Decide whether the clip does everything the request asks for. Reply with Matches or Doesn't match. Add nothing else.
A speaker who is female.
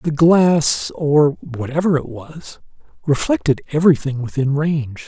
Doesn't match